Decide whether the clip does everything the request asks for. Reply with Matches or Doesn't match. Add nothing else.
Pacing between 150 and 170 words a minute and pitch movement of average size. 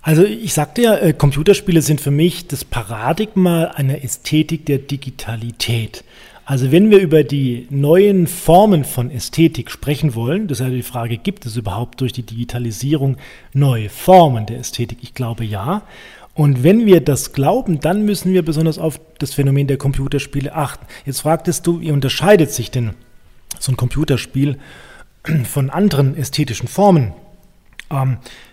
Matches